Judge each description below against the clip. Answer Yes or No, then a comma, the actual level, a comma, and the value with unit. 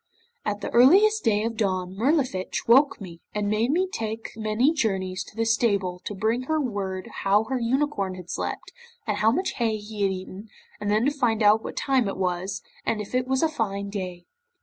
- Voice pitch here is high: Yes, high, 215 Hz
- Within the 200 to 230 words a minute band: Yes, fast, 205 wpm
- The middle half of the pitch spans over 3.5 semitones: Yes, average, 4.2 semitones